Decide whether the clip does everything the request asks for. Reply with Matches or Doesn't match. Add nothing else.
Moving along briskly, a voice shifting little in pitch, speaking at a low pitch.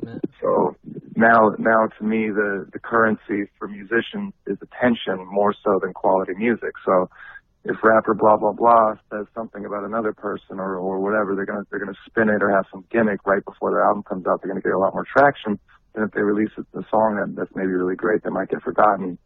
Matches